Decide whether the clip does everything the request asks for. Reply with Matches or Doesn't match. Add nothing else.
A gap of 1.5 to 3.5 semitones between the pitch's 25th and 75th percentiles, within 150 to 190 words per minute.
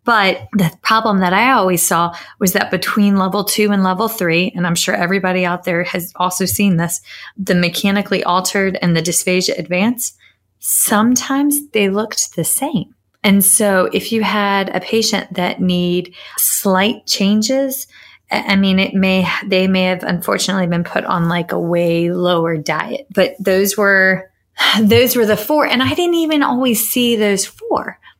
Matches